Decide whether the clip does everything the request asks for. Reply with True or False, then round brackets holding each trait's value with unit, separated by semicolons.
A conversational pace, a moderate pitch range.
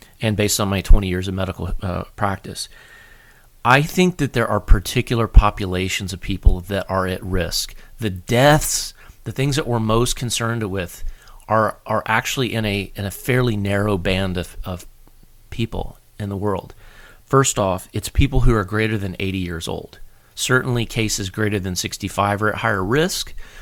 True (175 wpm; 3.4 semitones)